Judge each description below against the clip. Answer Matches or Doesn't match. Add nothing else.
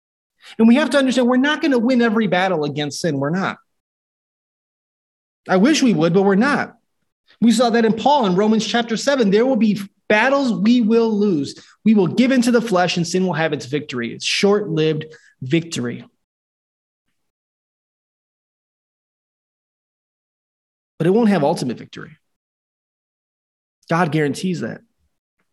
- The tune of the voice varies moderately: Doesn't match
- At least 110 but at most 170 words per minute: Matches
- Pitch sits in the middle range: Doesn't match